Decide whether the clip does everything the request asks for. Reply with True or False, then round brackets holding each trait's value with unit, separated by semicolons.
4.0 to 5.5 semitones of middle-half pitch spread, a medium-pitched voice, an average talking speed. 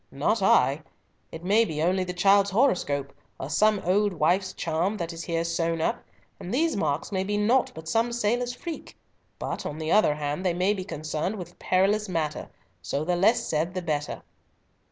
True (4.5 semitones; 180 Hz; 190 wpm)